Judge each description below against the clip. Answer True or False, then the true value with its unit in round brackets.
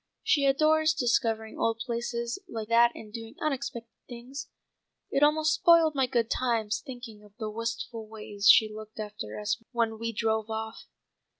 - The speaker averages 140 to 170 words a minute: True (160 wpm)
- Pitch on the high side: True (230 Hz)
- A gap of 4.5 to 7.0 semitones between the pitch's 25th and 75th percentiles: False (3.0 semitones)